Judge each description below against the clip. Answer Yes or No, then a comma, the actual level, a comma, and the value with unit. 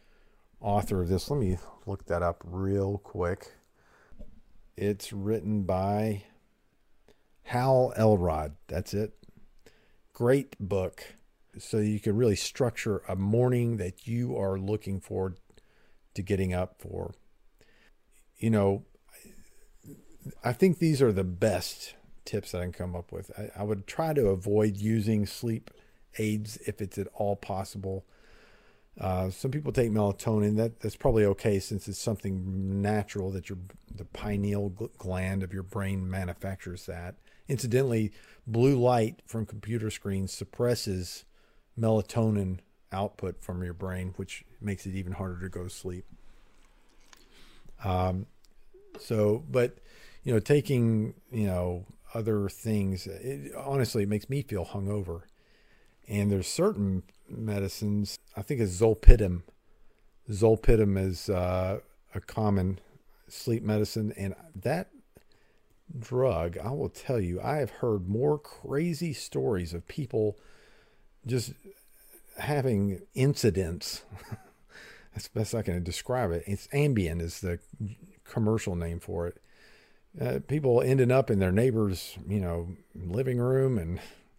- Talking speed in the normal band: No, slow, 130 wpm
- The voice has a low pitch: Yes, low, 105 Hz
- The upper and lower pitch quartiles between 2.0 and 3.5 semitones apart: Yes, average, 3.1 semitones